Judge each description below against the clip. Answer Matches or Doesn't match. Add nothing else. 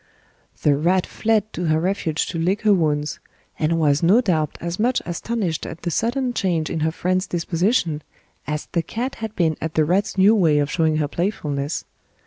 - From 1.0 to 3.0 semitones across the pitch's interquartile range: Doesn't match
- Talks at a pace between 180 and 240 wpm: Matches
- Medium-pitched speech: Matches